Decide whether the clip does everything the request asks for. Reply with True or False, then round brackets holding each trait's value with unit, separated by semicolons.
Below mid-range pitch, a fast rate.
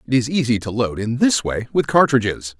True (120 Hz; 230 wpm)